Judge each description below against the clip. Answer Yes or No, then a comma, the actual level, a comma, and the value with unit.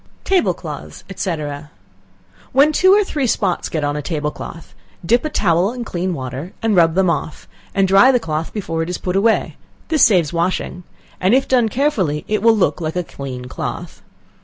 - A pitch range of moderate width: No, wide, 6.1 semitones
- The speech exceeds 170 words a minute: Yes, average, 190 wpm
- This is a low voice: No, medium, 185 Hz